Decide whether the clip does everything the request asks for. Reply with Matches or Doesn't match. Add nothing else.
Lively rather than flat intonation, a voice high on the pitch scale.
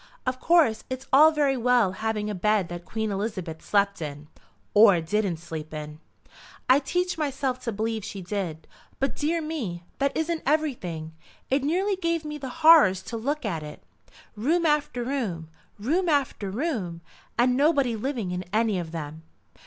Matches